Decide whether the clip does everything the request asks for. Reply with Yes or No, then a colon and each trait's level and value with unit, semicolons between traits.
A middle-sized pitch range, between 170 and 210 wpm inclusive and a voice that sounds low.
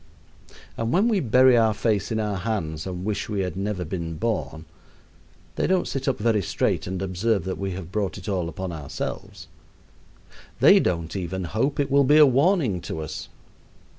Yes: average, 4.7 semitones; average, 185 wpm; low, 100 Hz